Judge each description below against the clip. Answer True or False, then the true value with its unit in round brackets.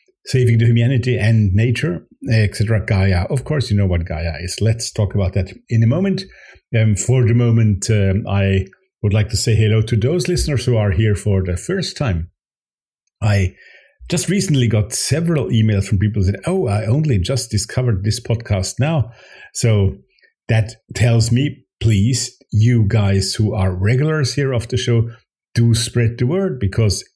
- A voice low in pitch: True (115 Hz)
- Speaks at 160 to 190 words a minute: True (175 wpm)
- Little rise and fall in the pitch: False (3.7 semitones)